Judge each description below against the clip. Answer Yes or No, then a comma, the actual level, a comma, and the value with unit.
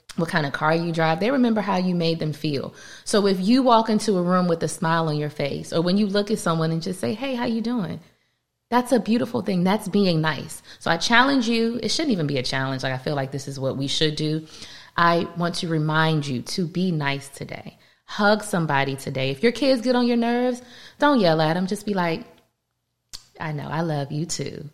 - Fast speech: Yes, fast, 240 wpm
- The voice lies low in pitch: No, medium, 170 Hz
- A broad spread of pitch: Yes, wide, 6.1 semitones